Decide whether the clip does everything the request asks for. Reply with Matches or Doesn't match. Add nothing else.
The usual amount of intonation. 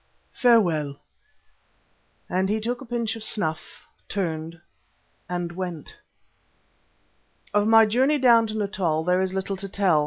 Matches